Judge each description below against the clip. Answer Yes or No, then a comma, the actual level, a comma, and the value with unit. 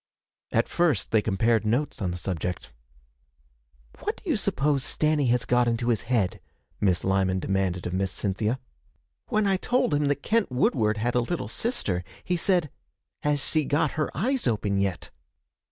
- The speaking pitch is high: No, low, 120 Hz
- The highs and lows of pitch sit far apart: Yes, wide, 7.3 semitones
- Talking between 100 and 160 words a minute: No, average, 170 wpm